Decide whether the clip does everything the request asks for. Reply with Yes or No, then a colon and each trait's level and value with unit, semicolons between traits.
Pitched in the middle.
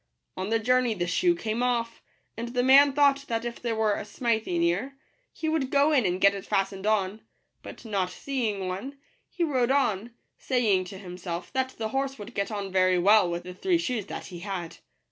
No: high, 220 Hz